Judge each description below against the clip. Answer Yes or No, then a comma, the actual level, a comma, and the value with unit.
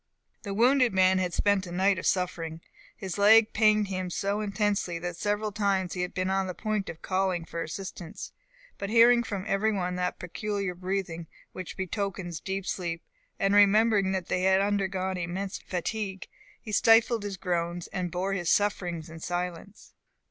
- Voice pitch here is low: No, high, 190 Hz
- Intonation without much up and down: Yes, narrow, 2.3 semitones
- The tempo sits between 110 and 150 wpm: No, average, 170 wpm